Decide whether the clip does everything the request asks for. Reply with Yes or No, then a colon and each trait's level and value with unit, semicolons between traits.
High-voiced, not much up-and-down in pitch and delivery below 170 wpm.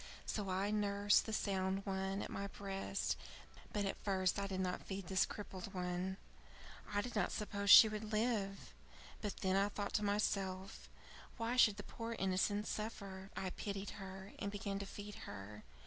No: high, 200 Hz; narrow, 1.5 semitones; average, 175 wpm